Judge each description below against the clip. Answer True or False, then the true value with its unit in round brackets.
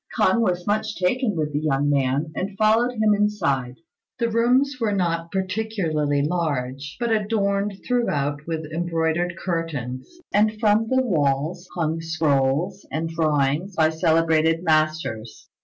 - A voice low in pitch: False (165 Hz)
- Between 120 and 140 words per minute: True (135 wpm)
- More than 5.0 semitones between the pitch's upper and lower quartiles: True (5.5 semitones)